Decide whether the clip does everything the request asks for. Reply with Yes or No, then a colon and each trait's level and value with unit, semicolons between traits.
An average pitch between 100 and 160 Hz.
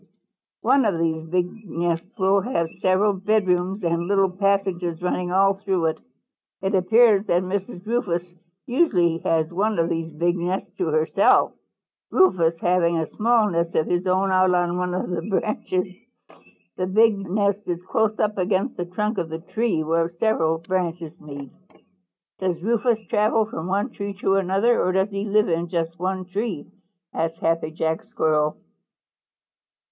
No: medium, 185 Hz